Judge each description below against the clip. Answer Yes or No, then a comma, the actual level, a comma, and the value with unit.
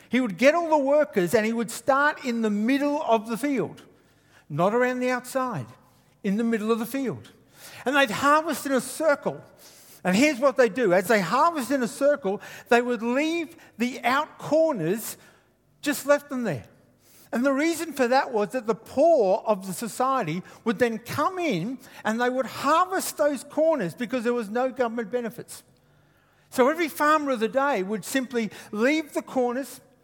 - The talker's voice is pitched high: Yes, very high, 255 Hz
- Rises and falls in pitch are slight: No, average, 4.2 semitones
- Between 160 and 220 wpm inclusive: Yes, average, 185 wpm